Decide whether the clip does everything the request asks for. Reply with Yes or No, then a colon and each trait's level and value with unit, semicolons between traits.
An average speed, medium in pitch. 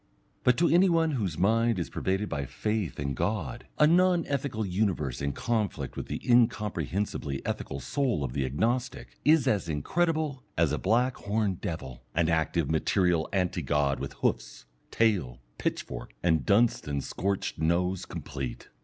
No: average, 155 wpm; very low, 95 Hz